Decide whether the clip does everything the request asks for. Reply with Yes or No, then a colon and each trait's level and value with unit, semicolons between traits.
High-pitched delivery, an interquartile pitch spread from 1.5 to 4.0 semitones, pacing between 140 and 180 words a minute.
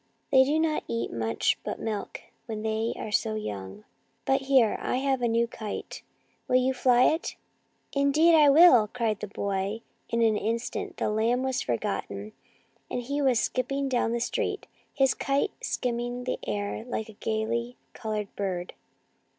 Yes: high, 235 Hz; average, 3.7 semitones; average, 175 wpm